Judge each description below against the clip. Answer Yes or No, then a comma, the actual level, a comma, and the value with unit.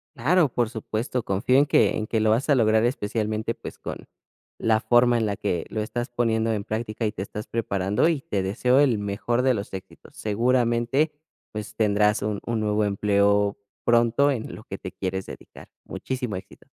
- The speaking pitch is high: No, low, 110 Hz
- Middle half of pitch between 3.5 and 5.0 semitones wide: No, average, 2.7 semitones